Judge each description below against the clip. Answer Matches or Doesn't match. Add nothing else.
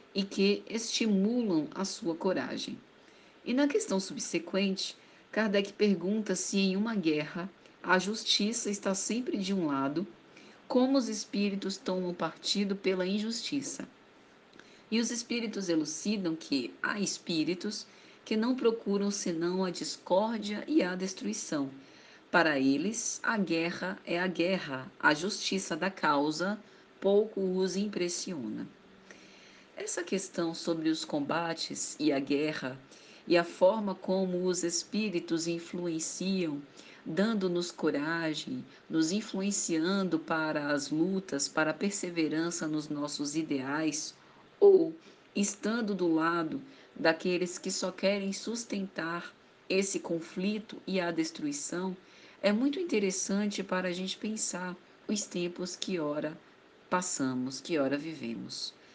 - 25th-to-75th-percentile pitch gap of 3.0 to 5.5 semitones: Matches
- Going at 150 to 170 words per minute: Doesn't match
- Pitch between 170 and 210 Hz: Matches